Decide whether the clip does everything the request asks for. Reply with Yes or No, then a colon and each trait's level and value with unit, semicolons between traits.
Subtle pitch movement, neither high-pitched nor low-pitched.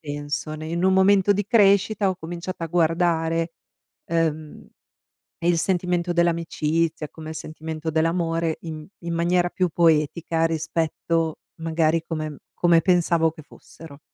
Yes: narrow, 1.6 semitones; medium, 165 Hz